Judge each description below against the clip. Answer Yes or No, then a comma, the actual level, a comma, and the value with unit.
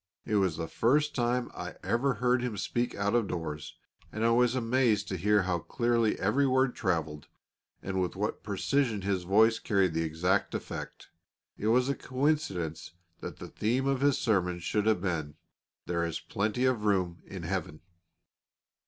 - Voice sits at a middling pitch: No, low, 105 Hz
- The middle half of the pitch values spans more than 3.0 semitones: Yes, wide, 5.4 semitones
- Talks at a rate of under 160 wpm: No, average, 170 wpm